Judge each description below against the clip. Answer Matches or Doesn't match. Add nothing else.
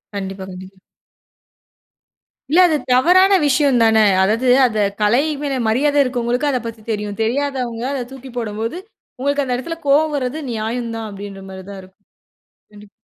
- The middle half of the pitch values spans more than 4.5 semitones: Matches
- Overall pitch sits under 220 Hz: Doesn't match